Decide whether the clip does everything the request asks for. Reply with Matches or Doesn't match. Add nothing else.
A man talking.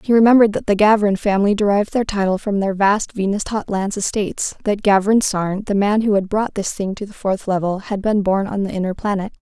Doesn't match